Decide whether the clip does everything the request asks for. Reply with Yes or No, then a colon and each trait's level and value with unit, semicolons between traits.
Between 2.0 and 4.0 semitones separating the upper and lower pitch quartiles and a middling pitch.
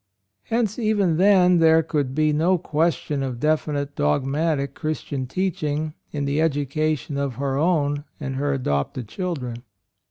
Yes: average, 3.0 semitones; medium, 150 Hz